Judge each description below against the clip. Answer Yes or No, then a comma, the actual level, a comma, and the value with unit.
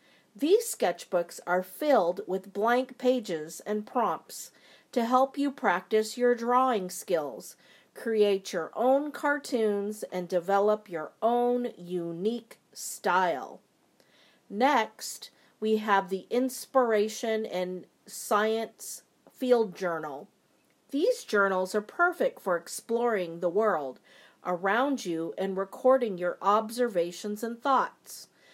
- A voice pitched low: No, high, 215 Hz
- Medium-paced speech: No, slow, 105 wpm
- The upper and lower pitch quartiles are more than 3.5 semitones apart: Yes, average, 5.1 semitones